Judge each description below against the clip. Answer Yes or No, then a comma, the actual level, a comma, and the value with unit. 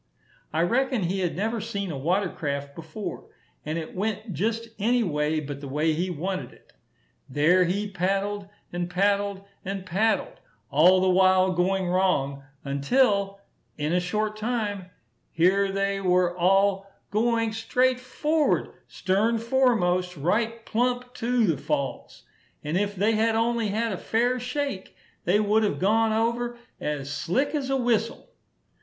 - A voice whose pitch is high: Yes, high, 195 Hz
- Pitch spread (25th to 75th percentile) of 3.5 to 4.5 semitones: Yes, average, 4.2 semitones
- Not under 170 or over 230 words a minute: No, average, 150 wpm